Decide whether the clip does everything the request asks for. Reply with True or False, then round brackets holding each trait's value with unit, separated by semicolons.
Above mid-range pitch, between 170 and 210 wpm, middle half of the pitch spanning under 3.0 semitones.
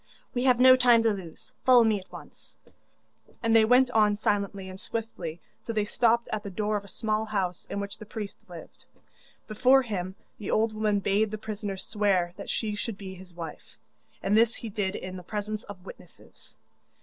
True (210 Hz; 195 wpm; 2.4 semitones)